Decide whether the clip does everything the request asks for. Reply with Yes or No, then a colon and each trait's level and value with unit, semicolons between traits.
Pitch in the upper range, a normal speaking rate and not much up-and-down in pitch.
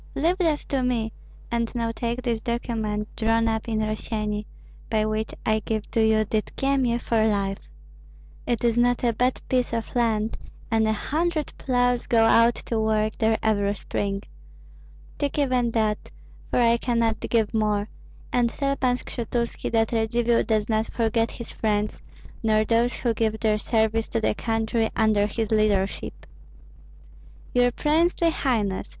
Yes: high, 225 Hz; average, 155 wpm; narrow, 1.9 semitones